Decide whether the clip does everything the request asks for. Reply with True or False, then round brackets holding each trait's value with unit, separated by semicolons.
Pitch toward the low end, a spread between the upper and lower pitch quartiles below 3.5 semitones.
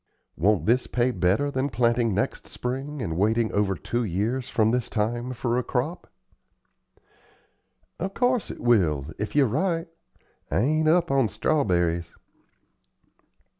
False (120 Hz; 4.8 semitones)